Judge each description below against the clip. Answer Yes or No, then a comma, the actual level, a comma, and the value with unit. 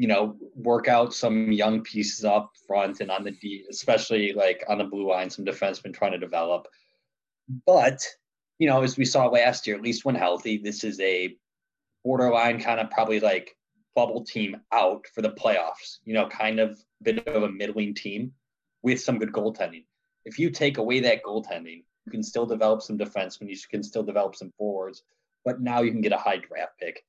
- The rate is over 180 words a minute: Yes, average, 200 wpm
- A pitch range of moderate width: Yes, average, 3.5 semitones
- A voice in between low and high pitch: No, low, 110 Hz